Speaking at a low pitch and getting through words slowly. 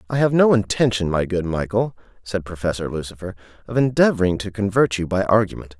No: low, 100 Hz; average, 175 wpm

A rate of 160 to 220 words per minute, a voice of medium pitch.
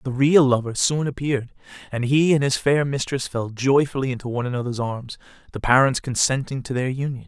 No: average, 190 wpm; low, 130 Hz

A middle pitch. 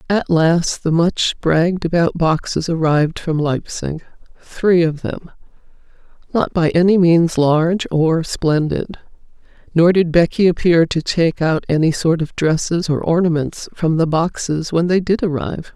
Yes: medium, 165 Hz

